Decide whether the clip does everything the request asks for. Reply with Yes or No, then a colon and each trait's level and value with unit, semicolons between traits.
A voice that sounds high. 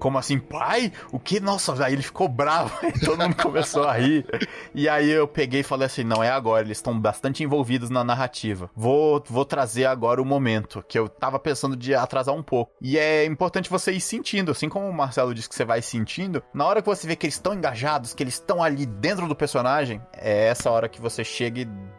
No: medium, 140 Hz